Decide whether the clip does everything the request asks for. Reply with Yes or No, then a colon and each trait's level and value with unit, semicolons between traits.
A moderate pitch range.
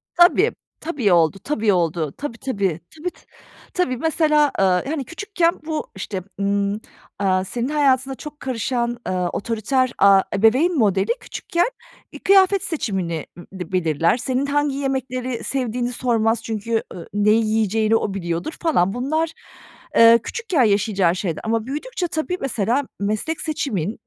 No: wide, 6.6 semitones